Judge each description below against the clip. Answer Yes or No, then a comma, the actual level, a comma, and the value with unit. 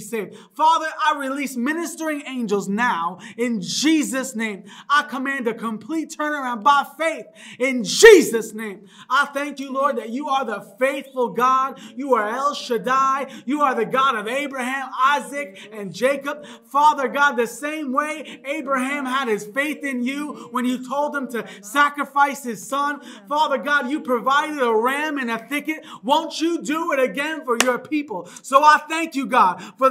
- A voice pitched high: Yes, very high, 270 Hz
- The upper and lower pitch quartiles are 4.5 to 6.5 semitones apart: No, average, 3.4 semitones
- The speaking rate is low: No, average, 170 wpm